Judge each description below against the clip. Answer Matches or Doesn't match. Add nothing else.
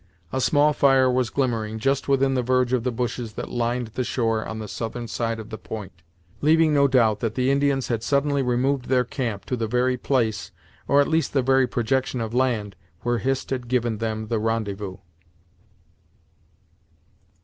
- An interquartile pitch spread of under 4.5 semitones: Matches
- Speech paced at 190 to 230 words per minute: Doesn't match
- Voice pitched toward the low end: Matches